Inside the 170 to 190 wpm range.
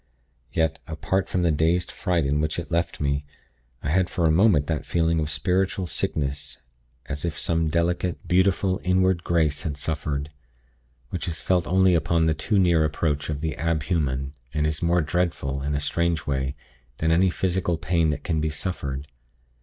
Yes: average, 180 wpm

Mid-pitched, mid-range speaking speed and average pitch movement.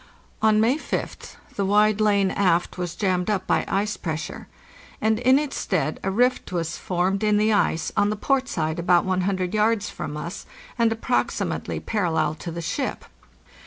No: high, 200 Hz; average, 170 wpm; average, 3.5 semitones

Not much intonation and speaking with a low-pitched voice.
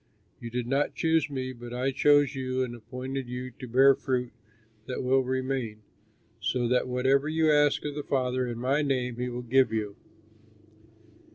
Yes: narrow, 1.7 semitones; low, 130 Hz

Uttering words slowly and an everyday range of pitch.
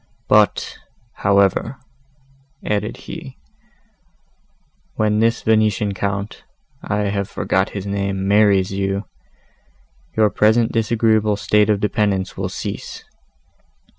No: slow, 100 wpm; narrow, 1.5 semitones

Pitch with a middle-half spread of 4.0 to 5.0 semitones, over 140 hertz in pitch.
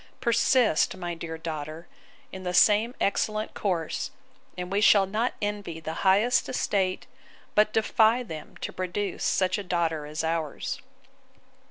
Yes: average, 4.4 semitones; high, 190 Hz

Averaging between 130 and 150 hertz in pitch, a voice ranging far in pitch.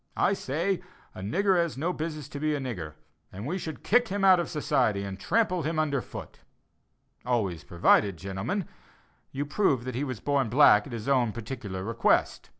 Yes: low, 135 Hz; wide, 7.8 semitones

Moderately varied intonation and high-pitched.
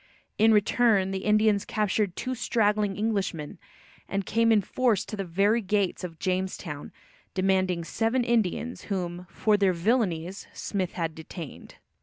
Yes: average, 3.1 semitones; high, 200 Hz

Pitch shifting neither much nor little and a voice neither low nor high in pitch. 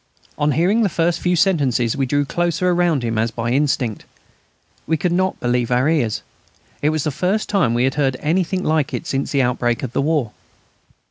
No: wide, 5.8 semitones; medium, 145 Hz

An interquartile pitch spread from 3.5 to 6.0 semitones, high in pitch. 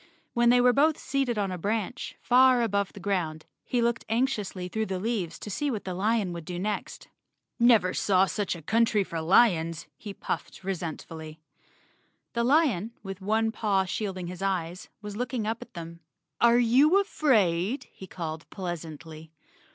Yes: average, 4.8 semitones; high, 200 Hz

